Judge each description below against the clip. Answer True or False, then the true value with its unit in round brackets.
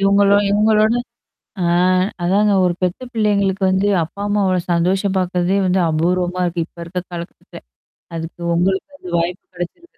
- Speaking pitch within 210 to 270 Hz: False (185 Hz)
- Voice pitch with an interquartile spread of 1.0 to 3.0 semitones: True (2.4 semitones)